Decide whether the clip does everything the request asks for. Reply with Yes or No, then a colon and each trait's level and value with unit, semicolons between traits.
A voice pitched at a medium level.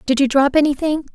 No: very high, 280 Hz